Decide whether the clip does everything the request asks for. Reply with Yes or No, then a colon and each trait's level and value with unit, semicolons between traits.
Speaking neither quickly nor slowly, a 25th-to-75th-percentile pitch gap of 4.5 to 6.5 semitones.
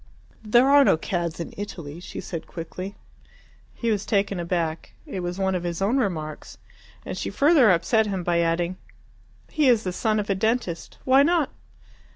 Yes: average, 180 wpm; average, 4.8 semitones